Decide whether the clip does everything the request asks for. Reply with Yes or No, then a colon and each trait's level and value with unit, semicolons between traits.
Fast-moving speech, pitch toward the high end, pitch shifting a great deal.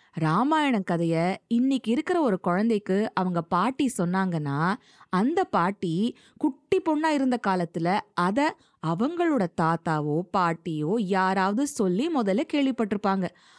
No: average, 100 wpm; high, 195 Hz; wide, 7.0 semitones